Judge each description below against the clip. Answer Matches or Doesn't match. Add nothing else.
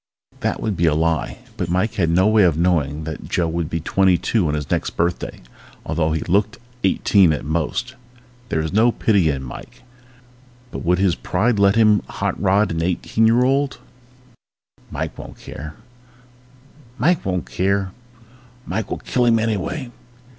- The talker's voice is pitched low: Matches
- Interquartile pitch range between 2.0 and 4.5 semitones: Doesn't match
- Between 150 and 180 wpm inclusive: Matches